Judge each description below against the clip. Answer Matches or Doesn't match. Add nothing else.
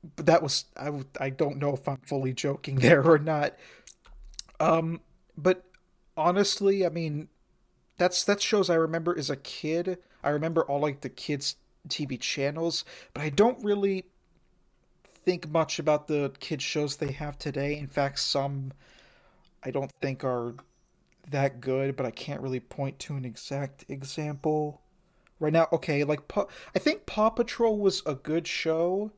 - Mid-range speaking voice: Matches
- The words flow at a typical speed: Matches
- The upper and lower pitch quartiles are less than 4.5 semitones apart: Matches